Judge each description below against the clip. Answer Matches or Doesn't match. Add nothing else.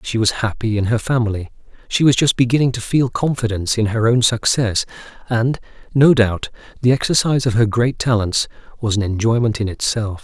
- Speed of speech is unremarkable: Matches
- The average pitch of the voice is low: Matches